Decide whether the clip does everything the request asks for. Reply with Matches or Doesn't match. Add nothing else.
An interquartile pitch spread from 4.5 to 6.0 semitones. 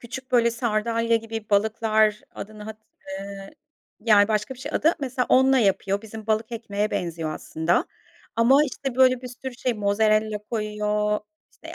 Doesn't match